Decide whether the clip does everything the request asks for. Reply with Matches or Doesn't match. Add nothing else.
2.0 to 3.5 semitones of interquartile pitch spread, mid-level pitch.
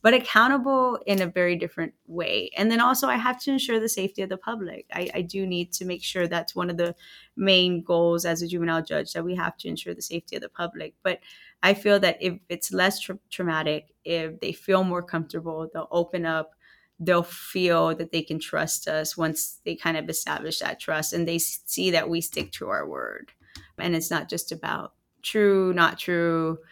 Matches